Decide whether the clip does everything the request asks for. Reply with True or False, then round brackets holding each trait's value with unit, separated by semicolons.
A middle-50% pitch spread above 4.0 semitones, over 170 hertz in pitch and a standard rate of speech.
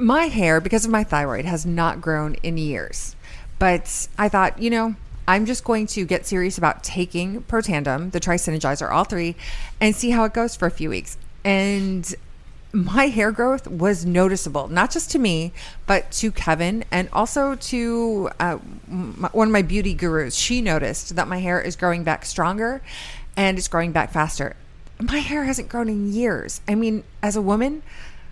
True (4.6 semitones; 190 Hz; 180 wpm)